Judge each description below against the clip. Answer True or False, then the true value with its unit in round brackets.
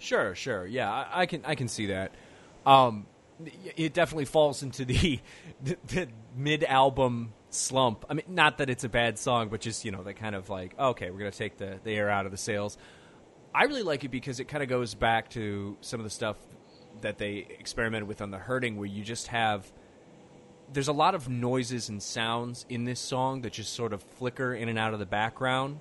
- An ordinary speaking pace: False (220 wpm)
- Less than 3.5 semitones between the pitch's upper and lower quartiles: False (4.3 semitones)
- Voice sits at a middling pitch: False (120 Hz)